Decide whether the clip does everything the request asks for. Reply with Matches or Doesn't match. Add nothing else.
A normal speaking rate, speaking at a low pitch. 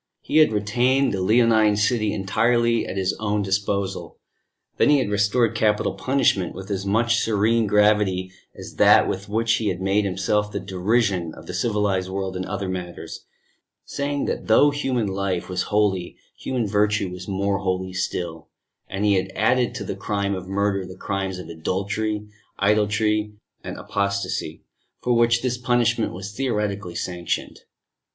Matches